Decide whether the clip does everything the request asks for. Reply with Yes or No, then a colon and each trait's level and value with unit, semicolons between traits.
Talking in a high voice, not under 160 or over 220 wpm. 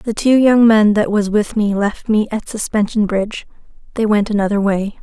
Yes: high, 210 Hz; fast, 205 wpm